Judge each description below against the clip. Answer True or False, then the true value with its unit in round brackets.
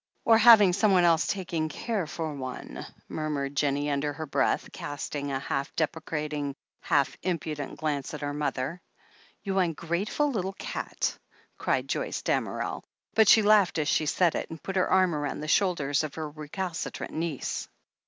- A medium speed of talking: True (165 wpm)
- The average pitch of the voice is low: False (155 Hz)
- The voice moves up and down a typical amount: True (4.3 semitones)